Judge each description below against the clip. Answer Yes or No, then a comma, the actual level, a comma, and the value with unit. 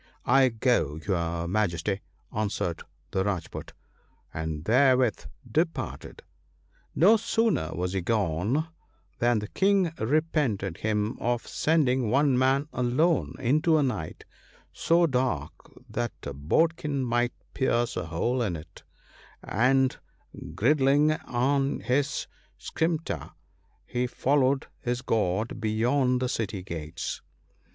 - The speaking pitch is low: Yes, low, 120 Hz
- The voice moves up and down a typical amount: No, wide, 6.2 semitones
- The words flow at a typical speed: No, slow, 120 wpm